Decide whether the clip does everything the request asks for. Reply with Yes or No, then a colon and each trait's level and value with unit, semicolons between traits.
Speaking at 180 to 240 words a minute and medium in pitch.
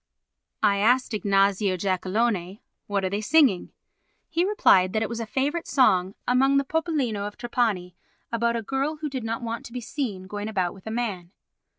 No: average, 185 wpm; high, 225 Hz